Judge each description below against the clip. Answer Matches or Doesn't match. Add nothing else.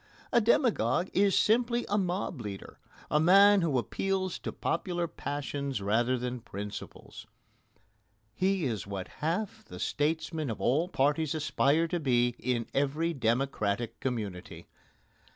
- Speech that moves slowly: Matches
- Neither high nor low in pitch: Matches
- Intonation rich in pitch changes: Matches